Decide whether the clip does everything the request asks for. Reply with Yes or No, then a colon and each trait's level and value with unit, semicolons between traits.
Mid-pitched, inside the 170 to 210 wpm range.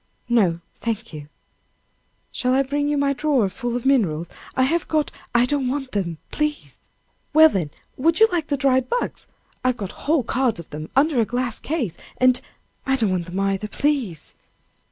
No: very high, 255 Hz; average, 190 wpm